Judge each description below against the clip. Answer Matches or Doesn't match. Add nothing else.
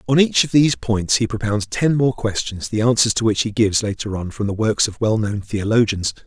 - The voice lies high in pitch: Doesn't match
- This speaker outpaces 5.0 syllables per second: Matches